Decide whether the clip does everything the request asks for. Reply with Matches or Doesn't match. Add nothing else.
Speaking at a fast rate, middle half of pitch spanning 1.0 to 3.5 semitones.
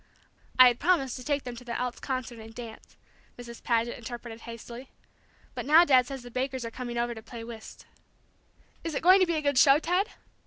Matches